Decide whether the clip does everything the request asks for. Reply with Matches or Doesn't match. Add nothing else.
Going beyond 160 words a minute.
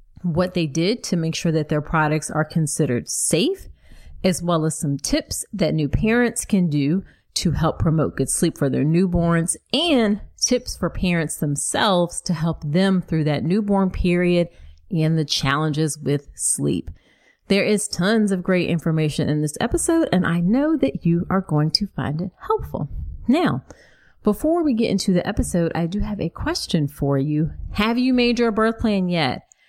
Matches